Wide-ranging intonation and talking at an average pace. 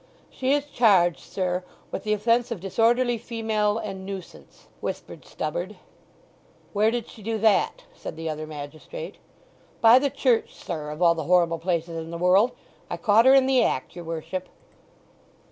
Yes: wide, 5.7 semitones; average, 160 wpm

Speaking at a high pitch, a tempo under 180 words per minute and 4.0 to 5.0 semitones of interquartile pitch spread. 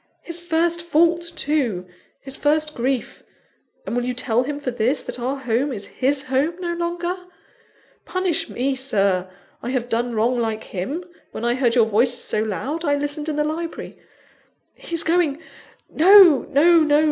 No: very high, 280 Hz; average, 170 wpm; wide, 5.4 semitones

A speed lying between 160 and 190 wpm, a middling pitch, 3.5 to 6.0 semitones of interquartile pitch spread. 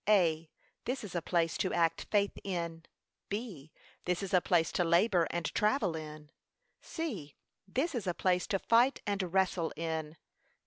Yes: average, 165 wpm; medium, 180 Hz; average, 3.8 semitones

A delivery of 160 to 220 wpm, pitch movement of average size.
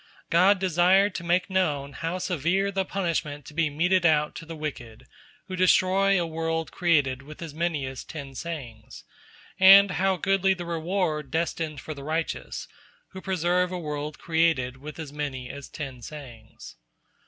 Yes: average, 165 wpm; average, 3.9 semitones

